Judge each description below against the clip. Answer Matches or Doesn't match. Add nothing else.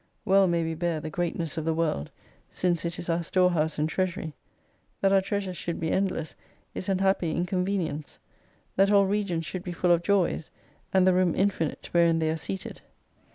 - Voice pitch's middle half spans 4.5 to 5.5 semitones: Doesn't match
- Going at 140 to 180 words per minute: Doesn't match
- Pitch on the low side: Doesn't match